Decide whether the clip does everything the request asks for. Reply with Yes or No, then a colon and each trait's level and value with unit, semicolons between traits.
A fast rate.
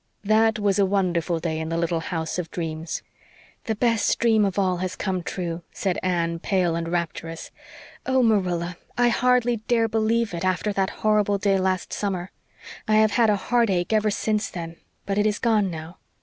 No: average, 185 wpm